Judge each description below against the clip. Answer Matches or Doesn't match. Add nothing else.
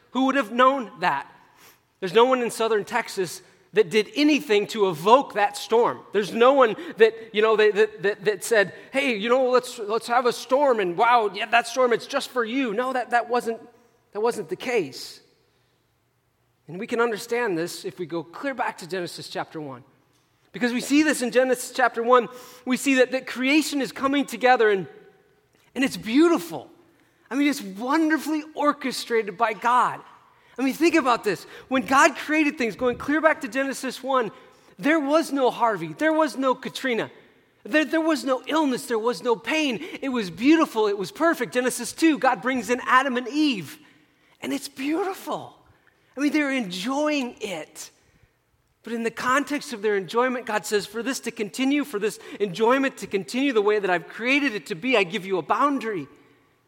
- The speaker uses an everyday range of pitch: Matches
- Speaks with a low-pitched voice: Doesn't match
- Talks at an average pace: Matches